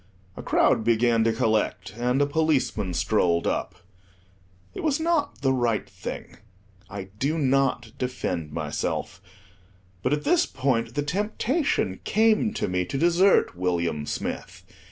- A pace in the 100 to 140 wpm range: Yes, slow, 135 wpm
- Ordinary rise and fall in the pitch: No, wide, 8.3 semitones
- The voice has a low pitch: Yes, low, 125 Hz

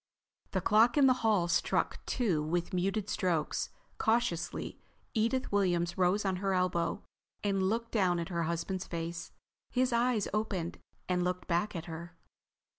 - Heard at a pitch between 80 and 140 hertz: No, medium, 185 Hz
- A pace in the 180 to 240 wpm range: No, average, 150 wpm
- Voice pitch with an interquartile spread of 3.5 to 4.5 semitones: Yes, average, 4.0 semitones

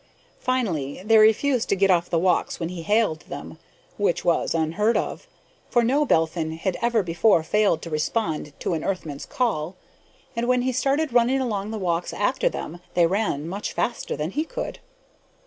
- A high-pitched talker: Yes, high, 195 Hz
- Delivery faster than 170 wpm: Yes, average, 180 wpm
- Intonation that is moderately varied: No, wide, 6.2 semitones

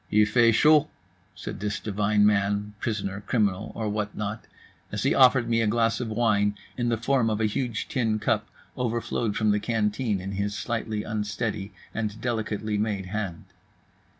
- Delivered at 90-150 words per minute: No, average, 170 wpm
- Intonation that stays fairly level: Yes, narrow, 1.9 semitones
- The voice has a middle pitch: No, low, 105 Hz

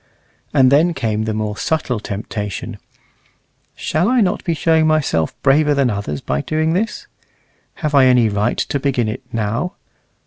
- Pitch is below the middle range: Yes, low, 130 Hz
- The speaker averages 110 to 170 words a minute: Yes, average, 160 wpm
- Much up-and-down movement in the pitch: Yes, wide, 6.5 semitones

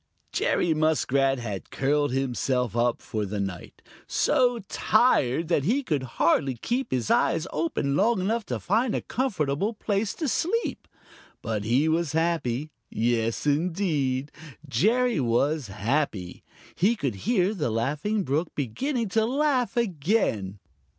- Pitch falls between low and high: Yes, medium, 150 Hz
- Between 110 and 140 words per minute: Yes, slow, 135 wpm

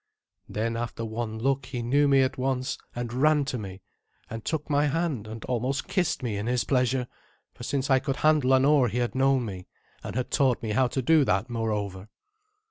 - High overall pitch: No, low, 125 Hz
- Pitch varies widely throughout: No, average, 3.3 semitones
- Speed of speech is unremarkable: No, fast, 210 wpm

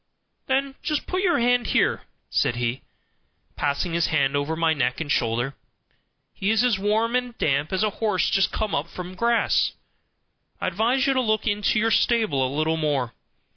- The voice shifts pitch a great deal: Yes, wide, 8.2 semitones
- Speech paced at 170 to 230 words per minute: Yes, average, 180 wpm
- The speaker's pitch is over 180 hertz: Yes, high, 190 Hz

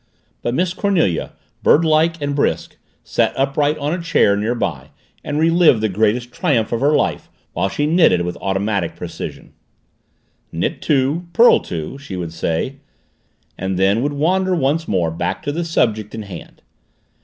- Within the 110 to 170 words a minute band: Yes, average, 160 wpm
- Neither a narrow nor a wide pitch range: No, wide, 8.2 semitones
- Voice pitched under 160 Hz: Yes, low, 135 Hz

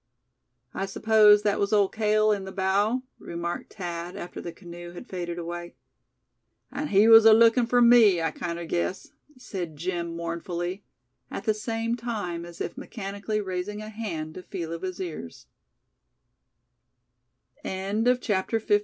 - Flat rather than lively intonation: No, average, 3.9 semitones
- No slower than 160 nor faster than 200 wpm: No, average, 145 wpm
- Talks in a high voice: Yes, high, 195 Hz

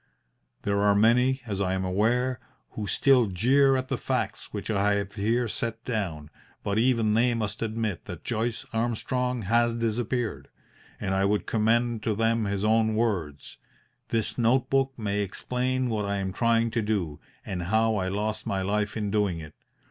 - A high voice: No, low, 110 Hz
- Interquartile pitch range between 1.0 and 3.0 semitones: Yes, average, 2.7 semitones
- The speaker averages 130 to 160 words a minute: No, average, 175 wpm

